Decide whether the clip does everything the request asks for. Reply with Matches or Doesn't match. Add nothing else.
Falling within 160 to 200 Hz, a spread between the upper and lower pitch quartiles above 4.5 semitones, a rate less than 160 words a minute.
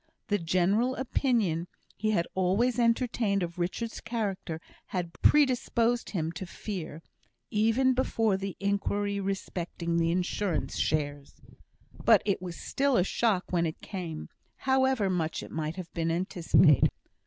Matches